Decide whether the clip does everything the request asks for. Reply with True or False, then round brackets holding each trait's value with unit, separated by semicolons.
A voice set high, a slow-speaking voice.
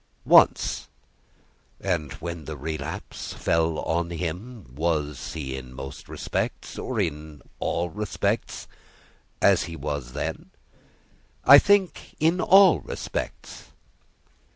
False (80 Hz; 105 wpm)